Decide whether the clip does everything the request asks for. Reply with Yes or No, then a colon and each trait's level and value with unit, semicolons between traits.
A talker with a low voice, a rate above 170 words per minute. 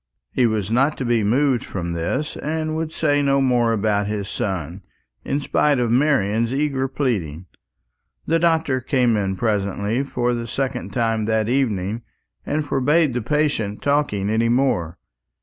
No: low, 120 Hz; average, 155 wpm